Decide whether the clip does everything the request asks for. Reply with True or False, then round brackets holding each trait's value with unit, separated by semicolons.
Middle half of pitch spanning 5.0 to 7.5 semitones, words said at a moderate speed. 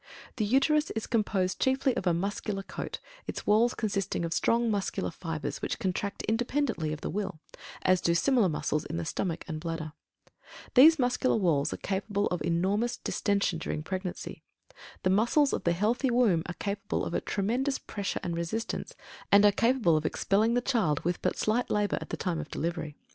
True (5.4 semitones; 185 wpm)